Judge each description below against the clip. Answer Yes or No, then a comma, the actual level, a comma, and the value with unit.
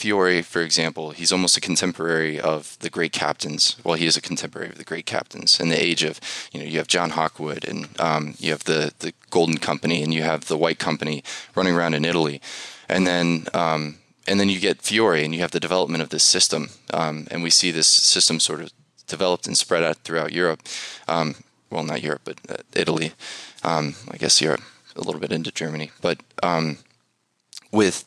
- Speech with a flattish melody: Yes, narrow, 1.8 semitones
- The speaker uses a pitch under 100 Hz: Yes, very low, 80 Hz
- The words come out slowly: No, fast, 205 wpm